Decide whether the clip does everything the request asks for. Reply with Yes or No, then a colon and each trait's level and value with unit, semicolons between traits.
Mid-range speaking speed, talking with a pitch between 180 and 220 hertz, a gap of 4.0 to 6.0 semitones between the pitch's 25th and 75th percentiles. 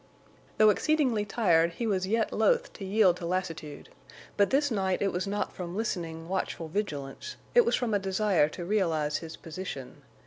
Yes: average, 175 wpm; high, 190 Hz; average, 4.3 semitones